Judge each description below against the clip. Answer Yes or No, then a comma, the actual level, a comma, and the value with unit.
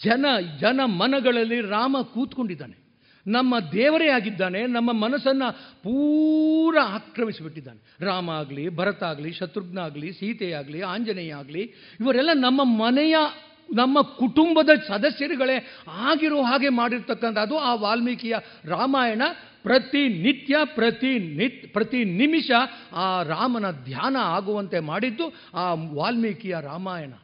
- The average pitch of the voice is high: Yes, high, 235 Hz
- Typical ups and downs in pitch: No, wide, 5.9 semitones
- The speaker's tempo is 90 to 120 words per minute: Yes, average, 100 wpm